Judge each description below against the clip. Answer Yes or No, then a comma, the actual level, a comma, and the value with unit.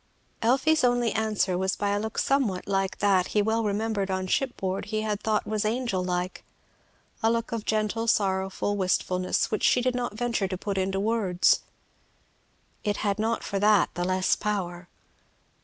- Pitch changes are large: No, average, 2.9 semitones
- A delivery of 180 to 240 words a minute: No, average, 170 wpm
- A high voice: Yes, high, 205 Hz